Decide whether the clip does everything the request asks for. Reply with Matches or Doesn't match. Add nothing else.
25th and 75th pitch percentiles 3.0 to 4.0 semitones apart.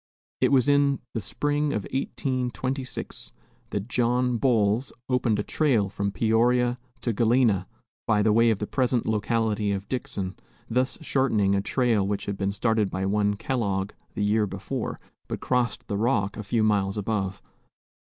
Matches